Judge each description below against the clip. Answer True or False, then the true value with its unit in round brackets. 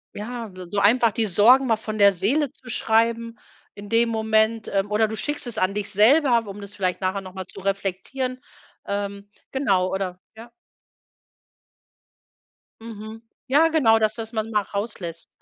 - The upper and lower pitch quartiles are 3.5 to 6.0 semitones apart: False (2.6 semitones)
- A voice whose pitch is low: False (215 Hz)